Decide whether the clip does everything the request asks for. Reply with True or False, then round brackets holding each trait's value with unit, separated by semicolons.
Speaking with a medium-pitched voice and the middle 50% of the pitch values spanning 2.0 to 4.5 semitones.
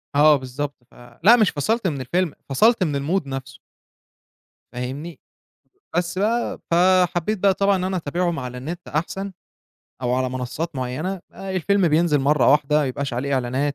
False (155 Hz; 5.6 semitones)